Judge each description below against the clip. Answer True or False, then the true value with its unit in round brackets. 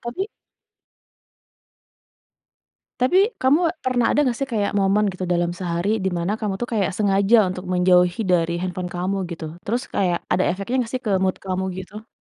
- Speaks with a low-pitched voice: False (195 Hz)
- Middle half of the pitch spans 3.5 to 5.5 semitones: True (4.0 semitones)